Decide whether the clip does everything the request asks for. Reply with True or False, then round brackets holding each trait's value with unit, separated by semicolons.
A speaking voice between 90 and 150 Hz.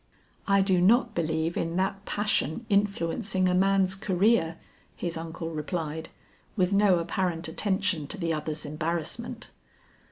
False (180 Hz)